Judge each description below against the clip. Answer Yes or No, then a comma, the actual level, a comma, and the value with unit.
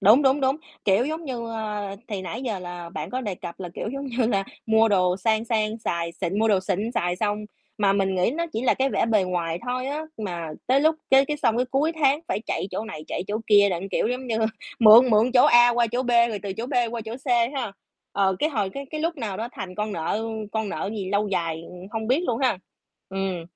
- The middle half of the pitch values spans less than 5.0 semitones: Yes, average, 4.5 semitones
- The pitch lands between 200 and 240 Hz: Yes, high, 220 Hz